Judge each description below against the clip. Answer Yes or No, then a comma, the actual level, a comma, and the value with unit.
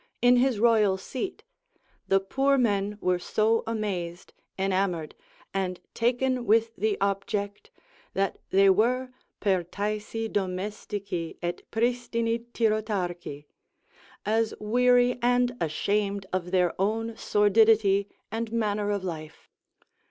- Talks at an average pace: No, slow, 105 wpm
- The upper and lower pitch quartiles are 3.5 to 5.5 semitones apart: No, average, 3.1 semitones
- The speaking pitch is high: Yes, high, 210 Hz